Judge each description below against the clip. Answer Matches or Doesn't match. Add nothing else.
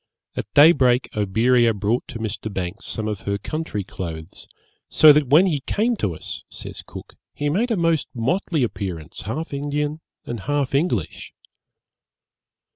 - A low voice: Matches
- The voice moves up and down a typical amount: Doesn't match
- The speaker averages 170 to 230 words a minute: Doesn't match